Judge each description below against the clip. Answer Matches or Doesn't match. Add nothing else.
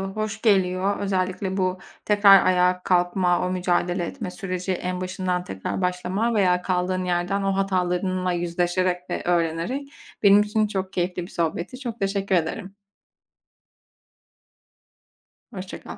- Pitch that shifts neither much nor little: Doesn't match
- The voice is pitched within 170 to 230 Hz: Matches